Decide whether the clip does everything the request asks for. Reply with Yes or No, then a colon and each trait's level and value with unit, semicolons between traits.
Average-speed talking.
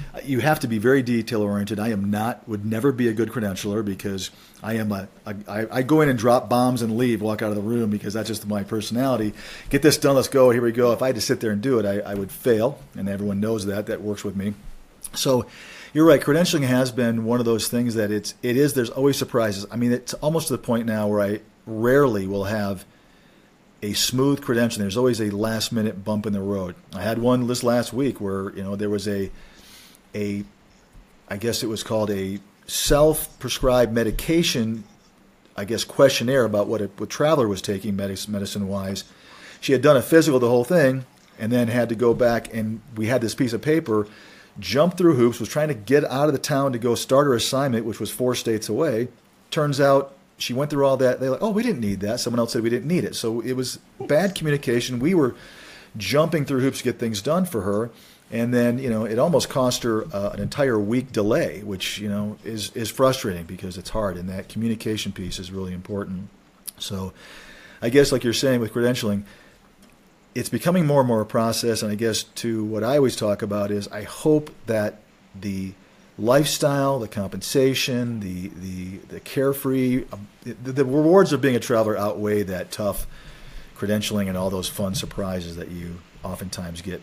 No: fast, 210 wpm